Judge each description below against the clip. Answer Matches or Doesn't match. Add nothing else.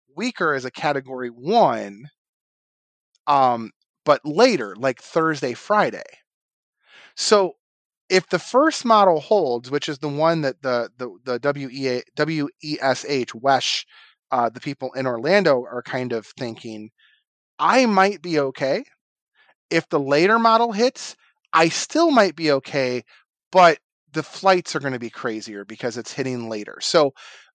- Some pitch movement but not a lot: Doesn't match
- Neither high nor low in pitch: Matches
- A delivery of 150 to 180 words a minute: Doesn't match